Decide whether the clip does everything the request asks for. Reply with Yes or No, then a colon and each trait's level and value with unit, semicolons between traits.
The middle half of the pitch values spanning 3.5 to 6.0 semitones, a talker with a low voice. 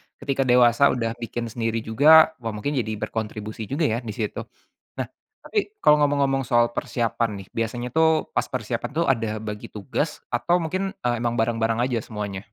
Yes: average, 4.1 semitones; low, 120 Hz